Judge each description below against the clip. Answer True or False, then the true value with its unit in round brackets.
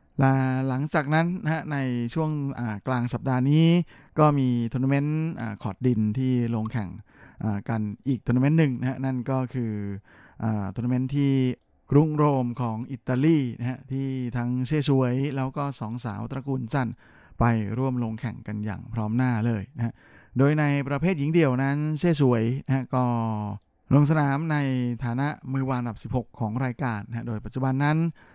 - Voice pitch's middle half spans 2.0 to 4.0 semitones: True (3.2 semitones)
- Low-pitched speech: True (130 Hz)